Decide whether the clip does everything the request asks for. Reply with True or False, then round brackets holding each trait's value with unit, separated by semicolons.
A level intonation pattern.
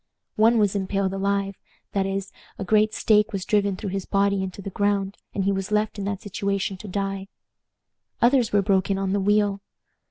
True (1.0 semitones)